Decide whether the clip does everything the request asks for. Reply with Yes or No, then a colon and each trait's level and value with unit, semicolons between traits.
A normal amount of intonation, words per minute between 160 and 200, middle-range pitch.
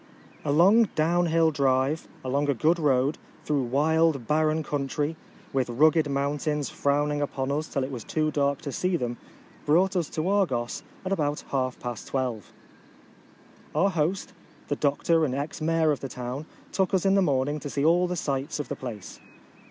Yes: average, 3.1 semitones; average, 180 wpm; medium, 145 Hz